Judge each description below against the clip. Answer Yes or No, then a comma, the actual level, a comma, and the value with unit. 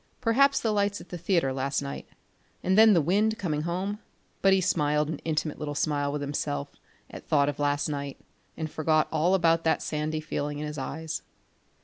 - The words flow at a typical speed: Yes, average, 195 wpm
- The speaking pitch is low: No, medium, 155 Hz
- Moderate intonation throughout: Yes, average, 4.1 semitones